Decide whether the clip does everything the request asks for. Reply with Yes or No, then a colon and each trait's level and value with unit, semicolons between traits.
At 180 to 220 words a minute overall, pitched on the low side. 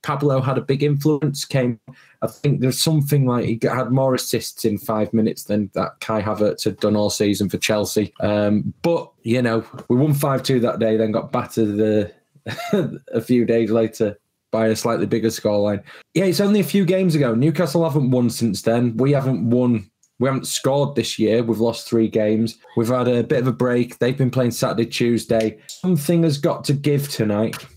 Yes: average, 200 wpm; low, 120 Hz